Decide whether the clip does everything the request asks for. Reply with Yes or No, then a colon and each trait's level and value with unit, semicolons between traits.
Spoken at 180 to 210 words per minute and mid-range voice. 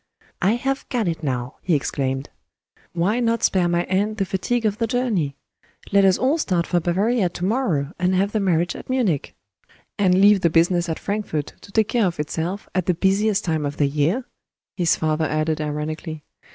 Yes: average, 190 wpm; medium, 180 Hz